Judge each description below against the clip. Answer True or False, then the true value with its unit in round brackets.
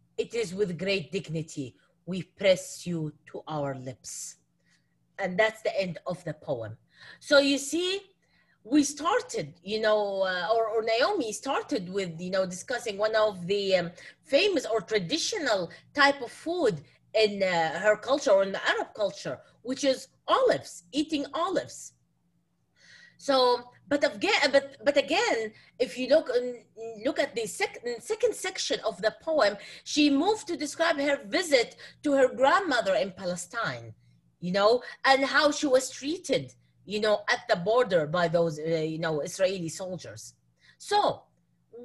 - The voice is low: False (220 Hz)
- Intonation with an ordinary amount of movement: False (8.0 semitones)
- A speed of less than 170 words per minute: True (145 wpm)